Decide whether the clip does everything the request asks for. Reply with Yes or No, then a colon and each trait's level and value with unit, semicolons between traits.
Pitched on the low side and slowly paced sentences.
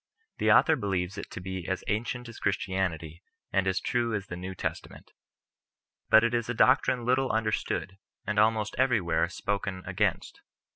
No: low, 105 Hz; average, 165 wpm